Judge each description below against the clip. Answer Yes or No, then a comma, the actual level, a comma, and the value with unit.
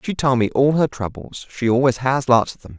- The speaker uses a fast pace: Yes, fast, 235 wpm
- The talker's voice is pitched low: Yes, low, 125 Hz